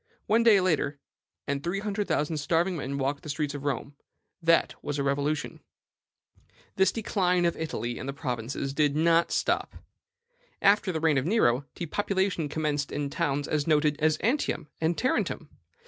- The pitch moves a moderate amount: Yes, average, 4.0 semitones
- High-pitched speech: No, medium, 155 Hz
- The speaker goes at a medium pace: Yes, average, 165 wpm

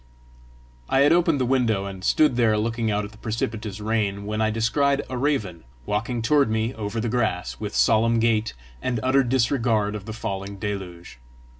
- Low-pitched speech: Yes, low, 110 Hz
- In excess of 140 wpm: Yes, average, 180 wpm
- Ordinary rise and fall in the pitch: Yes, average, 3.0 semitones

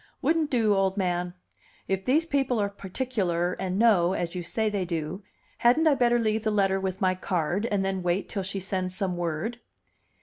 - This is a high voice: Yes, high, 195 Hz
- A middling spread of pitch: Yes, average, 3.8 semitones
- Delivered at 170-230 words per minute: Yes, average, 195 wpm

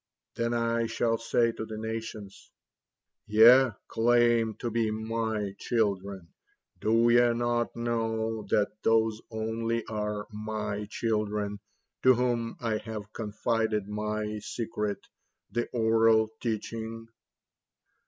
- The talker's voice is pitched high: No, low, 110 Hz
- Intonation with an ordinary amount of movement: No, narrow, 1.5 semitones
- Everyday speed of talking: No, slow, 110 wpm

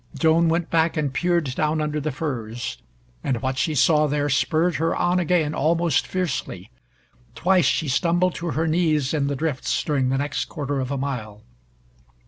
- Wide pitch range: No, average, 3.5 semitones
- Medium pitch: Yes, medium, 150 Hz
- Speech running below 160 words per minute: No, average, 175 wpm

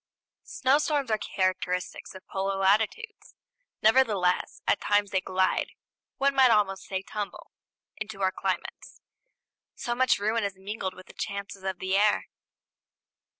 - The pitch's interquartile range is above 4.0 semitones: No, average, 2.9 semitones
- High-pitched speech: Yes, high, 200 Hz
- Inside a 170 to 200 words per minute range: No, slow, 135 wpm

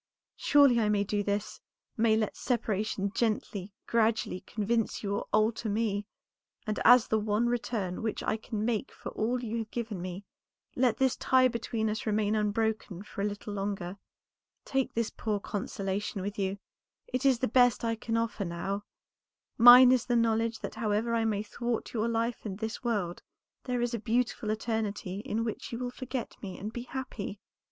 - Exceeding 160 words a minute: Yes, average, 180 wpm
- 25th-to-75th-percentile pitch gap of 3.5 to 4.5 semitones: No, narrow, 2.4 semitones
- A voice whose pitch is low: No, high, 220 Hz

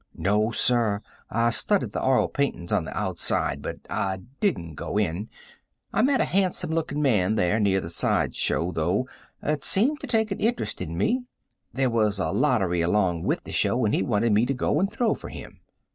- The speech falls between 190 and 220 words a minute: Yes, average, 200 wpm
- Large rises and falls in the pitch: Yes, wide, 8.1 semitones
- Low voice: Yes, low, 115 Hz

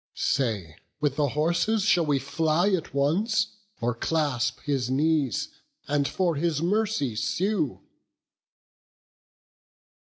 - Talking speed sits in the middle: No, slow, 105 wpm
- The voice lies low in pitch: No, medium, 150 Hz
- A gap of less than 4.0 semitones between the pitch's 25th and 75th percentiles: No, average, 4.3 semitones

